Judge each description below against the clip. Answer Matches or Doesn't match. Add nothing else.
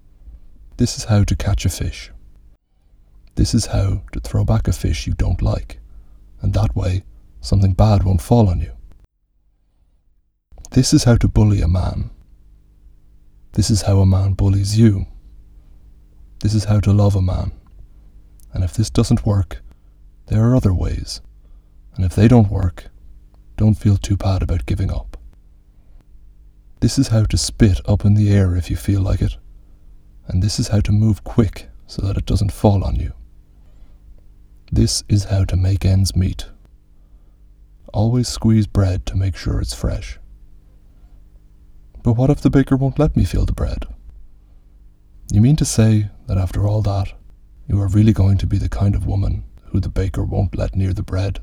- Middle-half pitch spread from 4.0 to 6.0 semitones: Matches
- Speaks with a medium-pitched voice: Doesn't match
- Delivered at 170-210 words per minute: Matches